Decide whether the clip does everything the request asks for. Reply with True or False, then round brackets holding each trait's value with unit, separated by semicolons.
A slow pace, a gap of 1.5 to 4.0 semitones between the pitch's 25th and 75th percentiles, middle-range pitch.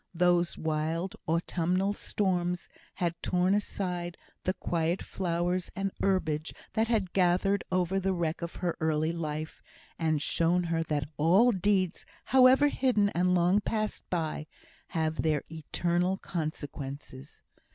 True (130 wpm; 2.9 semitones; 175 Hz)